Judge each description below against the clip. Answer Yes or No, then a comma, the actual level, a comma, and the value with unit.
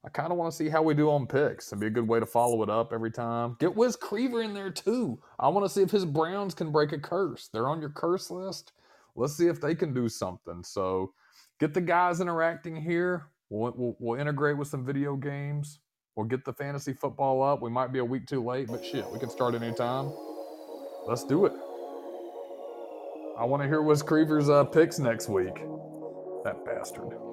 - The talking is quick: Yes, fast, 215 wpm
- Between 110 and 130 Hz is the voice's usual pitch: No, medium, 140 Hz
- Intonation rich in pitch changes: Yes, wide, 5.9 semitones